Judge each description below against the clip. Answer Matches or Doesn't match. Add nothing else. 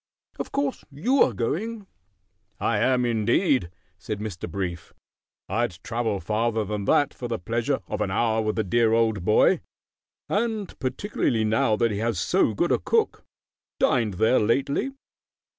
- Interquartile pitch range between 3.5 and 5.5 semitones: Matches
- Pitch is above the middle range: Doesn't match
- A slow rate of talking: Doesn't match